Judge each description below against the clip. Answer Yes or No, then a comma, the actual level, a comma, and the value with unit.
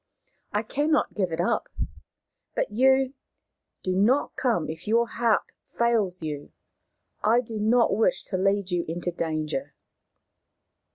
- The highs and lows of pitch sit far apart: No, average, 5.0 semitones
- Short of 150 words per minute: Yes, slow, 135 wpm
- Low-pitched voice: No, high, 210 Hz